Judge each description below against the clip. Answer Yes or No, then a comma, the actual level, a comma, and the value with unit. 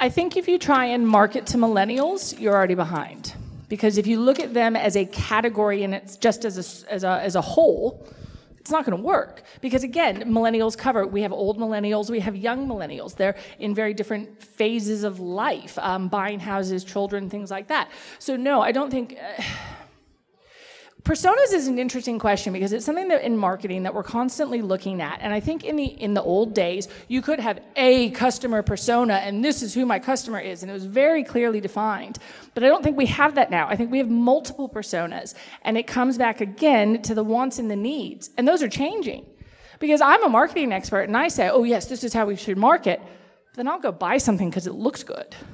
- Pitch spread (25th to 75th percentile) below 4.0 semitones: No, average, 4.6 semitones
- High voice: Yes, high, 225 Hz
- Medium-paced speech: No, fast, 220 wpm